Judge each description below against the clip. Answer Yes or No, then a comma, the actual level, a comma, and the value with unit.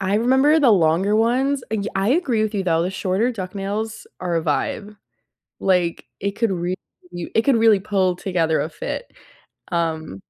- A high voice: Yes, high, 200 Hz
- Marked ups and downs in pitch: No, average, 4.0 semitones